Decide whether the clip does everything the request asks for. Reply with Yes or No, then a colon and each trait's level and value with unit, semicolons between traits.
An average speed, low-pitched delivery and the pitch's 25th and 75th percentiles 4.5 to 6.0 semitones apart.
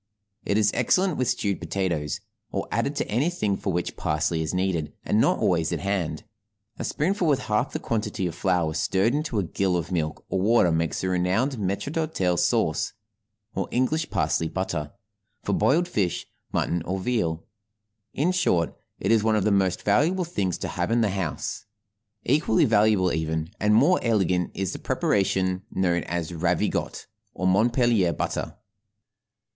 Yes: average, 165 wpm; very low, 95 Hz; average, 5.1 semitones